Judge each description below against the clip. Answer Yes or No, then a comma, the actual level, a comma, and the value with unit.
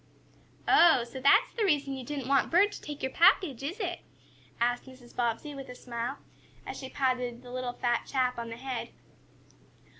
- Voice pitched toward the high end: Yes, very high, 260 Hz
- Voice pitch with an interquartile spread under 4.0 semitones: Yes, average, 3.2 semitones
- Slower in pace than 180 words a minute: No, average, 185 wpm